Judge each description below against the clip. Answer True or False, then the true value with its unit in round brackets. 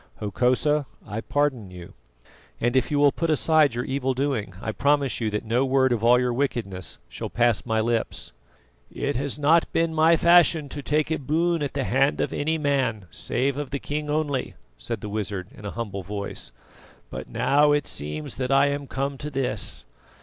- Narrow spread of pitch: False (4.5 semitones)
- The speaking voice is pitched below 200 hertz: True (135 Hz)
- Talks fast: False (195 wpm)